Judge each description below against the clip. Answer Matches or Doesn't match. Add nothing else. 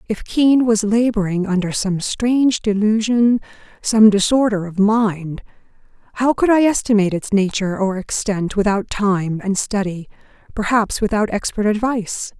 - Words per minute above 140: Doesn't match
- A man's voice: Doesn't match